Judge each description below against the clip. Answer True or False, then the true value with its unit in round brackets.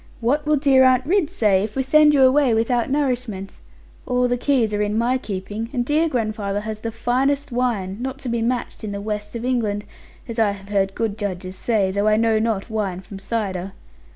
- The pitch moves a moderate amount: True (3.9 semitones)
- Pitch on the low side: False (225 Hz)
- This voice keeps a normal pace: False (210 wpm)